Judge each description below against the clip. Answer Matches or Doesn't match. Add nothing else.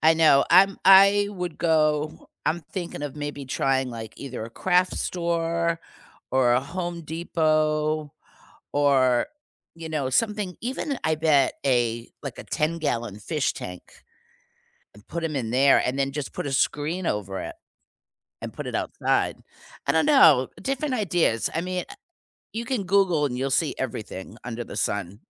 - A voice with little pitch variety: Doesn't match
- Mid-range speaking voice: Matches